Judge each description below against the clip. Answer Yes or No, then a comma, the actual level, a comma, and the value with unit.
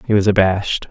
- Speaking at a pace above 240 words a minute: No, average, 200 wpm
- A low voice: Yes, low, 100 Hz